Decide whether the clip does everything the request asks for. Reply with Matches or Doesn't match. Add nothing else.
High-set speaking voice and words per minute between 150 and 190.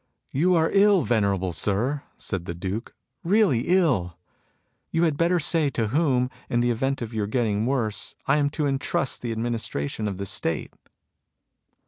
Doesn't match